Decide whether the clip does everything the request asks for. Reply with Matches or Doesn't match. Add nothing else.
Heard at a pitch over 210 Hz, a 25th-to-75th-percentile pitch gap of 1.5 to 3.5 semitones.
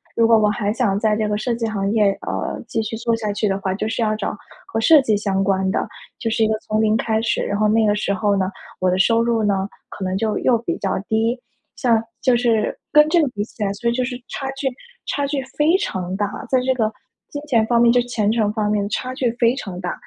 Matches